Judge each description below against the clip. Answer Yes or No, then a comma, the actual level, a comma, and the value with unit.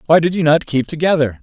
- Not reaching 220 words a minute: No, fast, 250 wpm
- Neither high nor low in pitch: Yes, medium, 155 Hz